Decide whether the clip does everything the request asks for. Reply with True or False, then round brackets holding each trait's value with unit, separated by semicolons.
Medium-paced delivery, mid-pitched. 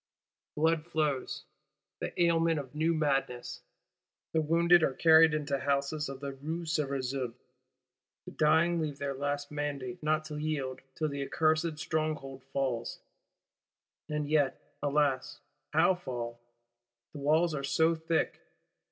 False (130 wpm; 150 Hz)